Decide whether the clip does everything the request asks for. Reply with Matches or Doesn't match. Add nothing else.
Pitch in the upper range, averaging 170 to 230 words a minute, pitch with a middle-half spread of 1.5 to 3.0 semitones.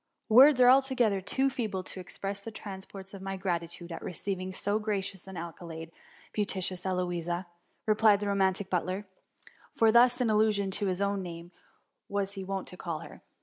Matches